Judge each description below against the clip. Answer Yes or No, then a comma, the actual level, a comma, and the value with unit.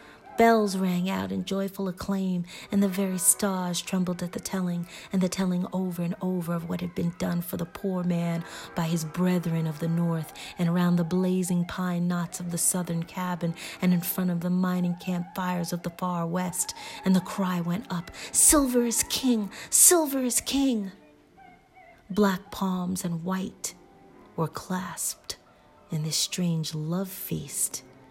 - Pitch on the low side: No, medium, 180 Hz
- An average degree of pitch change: No, narrow, 1.9 semitones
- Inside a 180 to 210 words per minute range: No, average, 170 wpm